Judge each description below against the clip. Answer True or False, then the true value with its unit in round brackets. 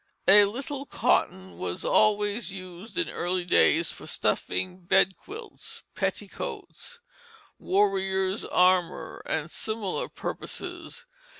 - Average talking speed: False (95 wpm)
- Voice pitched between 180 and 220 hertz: True (190 Hz)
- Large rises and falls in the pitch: False (2.9 semitones)